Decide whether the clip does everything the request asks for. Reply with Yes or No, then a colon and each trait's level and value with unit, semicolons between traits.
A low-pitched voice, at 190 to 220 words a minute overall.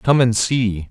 Yes: low, 115 Hz; average, 200 wpm